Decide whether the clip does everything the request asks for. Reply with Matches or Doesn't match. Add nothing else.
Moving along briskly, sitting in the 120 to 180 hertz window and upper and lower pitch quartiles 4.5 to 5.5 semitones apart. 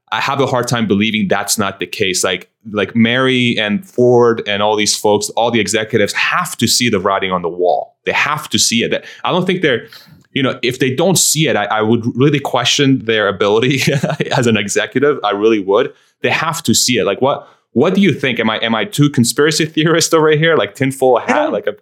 Matches